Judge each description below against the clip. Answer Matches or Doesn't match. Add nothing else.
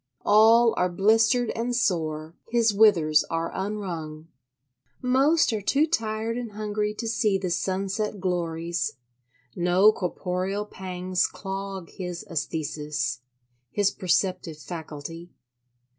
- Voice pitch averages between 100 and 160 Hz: Doesn't match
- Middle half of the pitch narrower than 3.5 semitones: Doesn't match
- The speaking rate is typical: Doesn't match